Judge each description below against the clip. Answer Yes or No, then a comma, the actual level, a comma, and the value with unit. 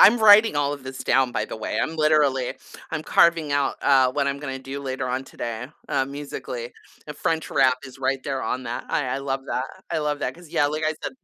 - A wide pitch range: No, narrow, 2.4 semitones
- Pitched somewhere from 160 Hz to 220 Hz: No, medium, 140 Hz